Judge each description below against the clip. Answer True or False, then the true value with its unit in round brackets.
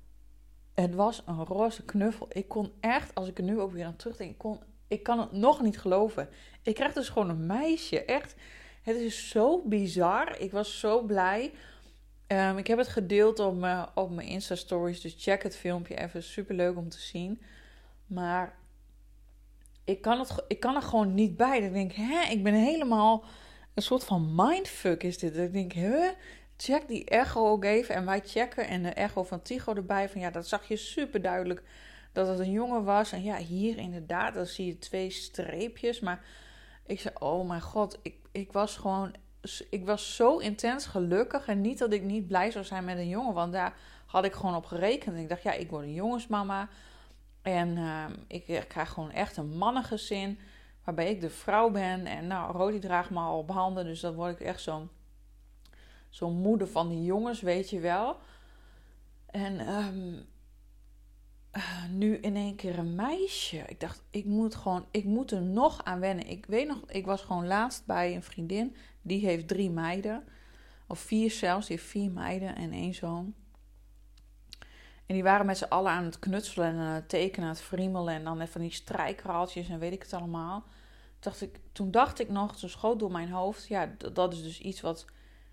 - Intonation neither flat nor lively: True (3.5 semitones)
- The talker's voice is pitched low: False (190 Hz)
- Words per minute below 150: False (200 wpm)